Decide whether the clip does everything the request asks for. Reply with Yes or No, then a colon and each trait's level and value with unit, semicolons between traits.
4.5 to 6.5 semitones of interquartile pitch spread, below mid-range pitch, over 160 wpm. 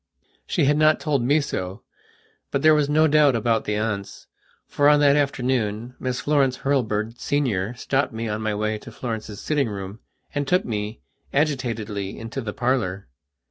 Yes: average, 5.0 semitones; low, 125 Hz; average, 170 wpm